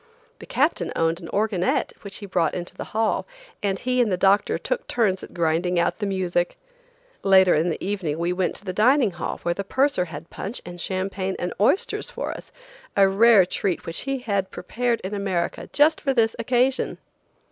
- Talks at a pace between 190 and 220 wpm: Yes, average, 195 wpm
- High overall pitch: Yes, high, 195 Hz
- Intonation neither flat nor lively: Yes, average, 4.1 semitones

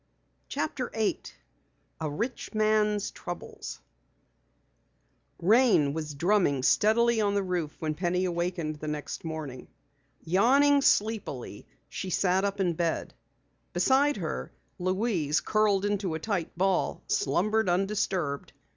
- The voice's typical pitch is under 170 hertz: No, medium, 185 Hz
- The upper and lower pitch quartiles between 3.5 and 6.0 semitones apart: Yes, average, 4.9 semitones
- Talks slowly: Yes, slow, 110 wpm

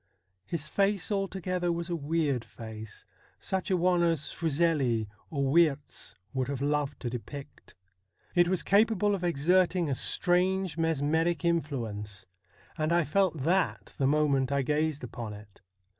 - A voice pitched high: No, medium, 160 Hz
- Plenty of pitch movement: No, average, 4.4 semitones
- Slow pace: No, average, 145 wpm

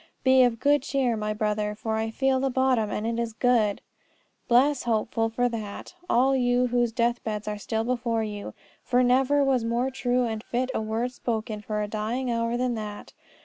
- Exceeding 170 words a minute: Yes, average, 190 wpm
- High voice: Yes, high, 235 Hz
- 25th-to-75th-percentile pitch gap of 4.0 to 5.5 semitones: No, narrow, 2.4 semitones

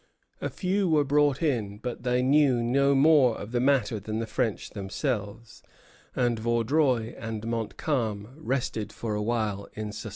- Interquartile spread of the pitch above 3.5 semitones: Yes, average, 4.1 semitones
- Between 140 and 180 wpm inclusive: Yes, average, 160 wpm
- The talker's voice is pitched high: No, low, 120 Hz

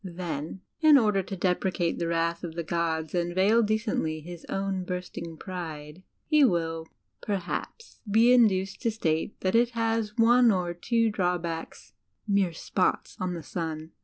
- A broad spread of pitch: No, average, 4.2 semitones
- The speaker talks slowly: No, average, 155 wpm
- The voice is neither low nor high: Yes, medium, 180 Hz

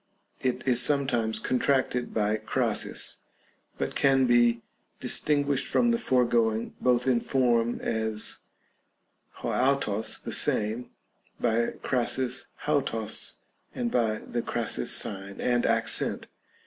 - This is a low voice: Yes, low, 120 Hz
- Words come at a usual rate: No, slow, 110 wpm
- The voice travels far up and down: No, average, 2.7 semitones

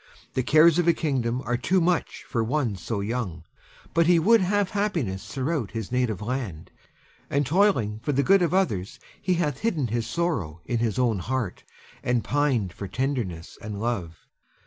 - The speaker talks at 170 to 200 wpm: Yes, average, 175 wpm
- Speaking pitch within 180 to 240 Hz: No, low, 125 Hz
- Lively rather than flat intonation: Yes, wide, 7.5 semitones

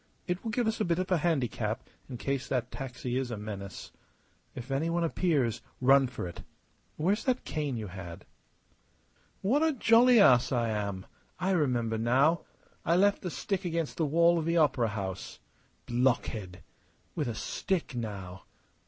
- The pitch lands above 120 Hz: Yes, low, 135 Hz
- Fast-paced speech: No, average, 170 wpm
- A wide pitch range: Yes, wide, 7.1 semitones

